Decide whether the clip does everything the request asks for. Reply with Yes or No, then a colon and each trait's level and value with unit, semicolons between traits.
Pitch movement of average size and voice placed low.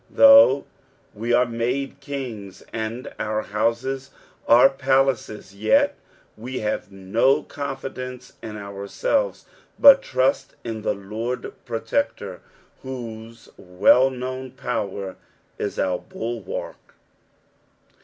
Yes: average, 3.8 semitones; low, 120 Hz